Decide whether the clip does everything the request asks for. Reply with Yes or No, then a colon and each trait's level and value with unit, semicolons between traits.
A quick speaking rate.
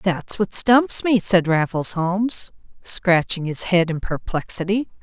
No: average, 145 wpm